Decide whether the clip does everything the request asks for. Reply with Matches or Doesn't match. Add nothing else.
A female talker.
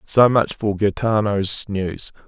Doesn't match